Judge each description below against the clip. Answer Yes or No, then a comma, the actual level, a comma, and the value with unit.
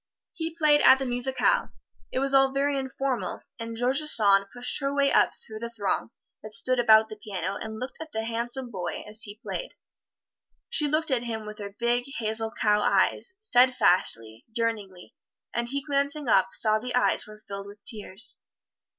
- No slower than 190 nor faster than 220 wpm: No, average, 180 wpm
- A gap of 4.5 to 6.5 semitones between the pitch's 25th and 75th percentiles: No, average, 4.1 semitones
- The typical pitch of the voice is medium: No, high, 235 Hz